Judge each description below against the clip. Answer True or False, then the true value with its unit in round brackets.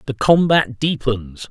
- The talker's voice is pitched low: True (130 Hz)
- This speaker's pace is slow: True (120 wpm)